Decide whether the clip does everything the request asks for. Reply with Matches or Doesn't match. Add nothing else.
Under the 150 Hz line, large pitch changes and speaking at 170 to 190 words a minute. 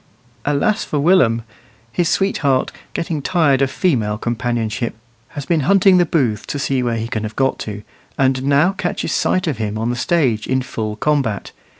Matches